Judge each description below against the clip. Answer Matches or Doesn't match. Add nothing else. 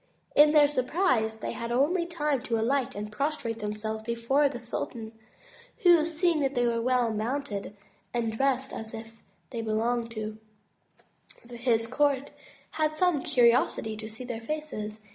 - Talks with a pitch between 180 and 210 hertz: Doesn't match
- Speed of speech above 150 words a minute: Doesn't match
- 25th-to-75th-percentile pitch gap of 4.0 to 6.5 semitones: Matches